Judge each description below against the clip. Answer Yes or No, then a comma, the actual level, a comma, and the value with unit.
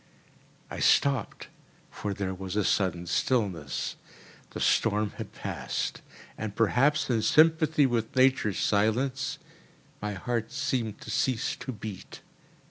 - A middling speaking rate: No, slow, 125 wpm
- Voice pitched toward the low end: Yes, low, 110 Hz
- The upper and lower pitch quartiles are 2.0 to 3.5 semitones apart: No, average, 4.5 semitones